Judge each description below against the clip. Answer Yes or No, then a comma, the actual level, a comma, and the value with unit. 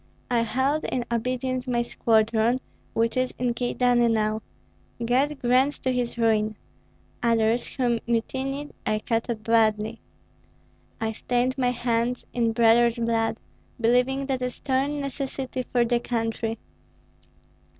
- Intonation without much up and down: Yes, narrow, 2.1 semitones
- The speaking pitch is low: No, high, 240 Hz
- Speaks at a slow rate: Yes, slow, 130 wpm